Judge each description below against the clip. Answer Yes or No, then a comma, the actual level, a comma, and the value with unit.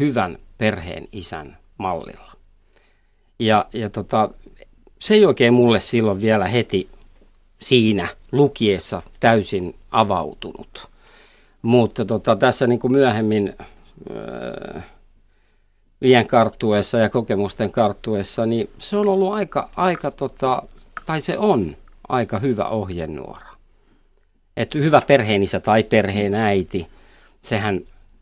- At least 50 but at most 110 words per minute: Yes, average, 100 wpm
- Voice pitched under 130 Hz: Yes, low, 115 Hz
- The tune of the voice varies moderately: Yes, average, 4.4 semitones